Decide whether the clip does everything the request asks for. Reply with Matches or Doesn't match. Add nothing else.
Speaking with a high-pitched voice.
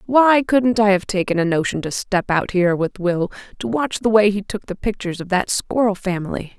Matches